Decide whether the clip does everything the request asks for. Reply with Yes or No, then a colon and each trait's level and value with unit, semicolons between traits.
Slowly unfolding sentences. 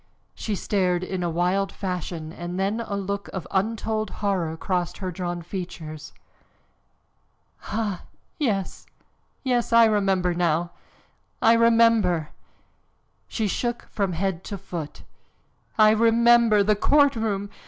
Yes: slow, 120 wpm